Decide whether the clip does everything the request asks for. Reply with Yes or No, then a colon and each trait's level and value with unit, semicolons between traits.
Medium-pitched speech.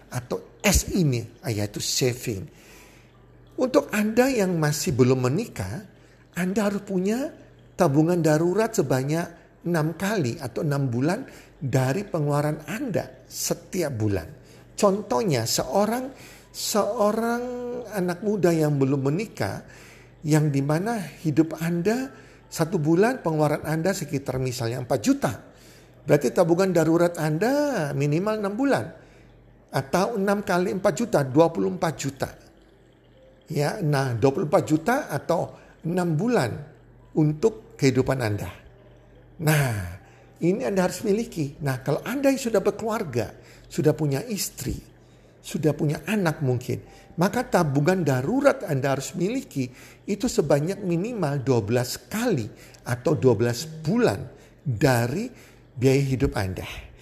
Yes: medium, 155 Hz